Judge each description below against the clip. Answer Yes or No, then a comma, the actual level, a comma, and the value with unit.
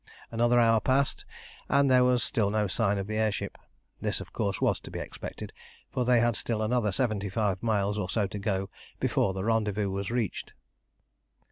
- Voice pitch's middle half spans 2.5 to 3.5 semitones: Yes, average, 3.0 semitones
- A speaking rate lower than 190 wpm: No, average, 195 wpm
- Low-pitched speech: Yes, low, 110 Hz